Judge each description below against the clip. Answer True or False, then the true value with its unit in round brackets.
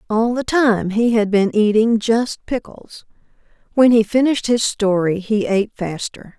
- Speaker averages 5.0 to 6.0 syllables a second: False (4.4 syllables/s)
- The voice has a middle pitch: False (220 Hz)